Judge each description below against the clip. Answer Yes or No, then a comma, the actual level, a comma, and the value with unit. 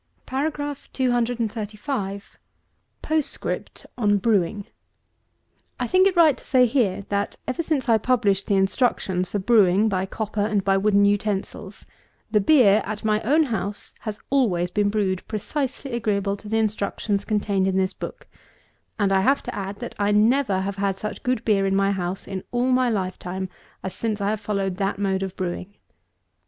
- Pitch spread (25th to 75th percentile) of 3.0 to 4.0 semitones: Yes, average, 3.4 semitones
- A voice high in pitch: Yes, high, 205 Hz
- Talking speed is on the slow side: No, average, 170 wpm